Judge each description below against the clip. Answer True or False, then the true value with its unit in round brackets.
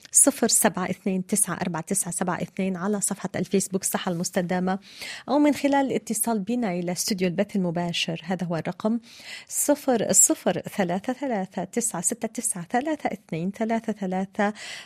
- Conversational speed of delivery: False (145 wpm)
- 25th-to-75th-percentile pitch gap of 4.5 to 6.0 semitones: False (4.0 semitones)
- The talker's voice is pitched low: False (200 Hz)